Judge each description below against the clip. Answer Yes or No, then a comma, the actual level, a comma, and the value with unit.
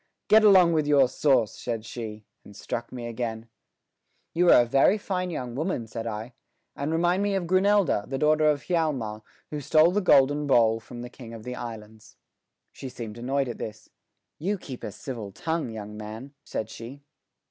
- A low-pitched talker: Yes, low, 130 Hz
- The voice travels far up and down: Yes, wide, 6.0 semitones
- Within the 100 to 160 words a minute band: No, average, 185 wpm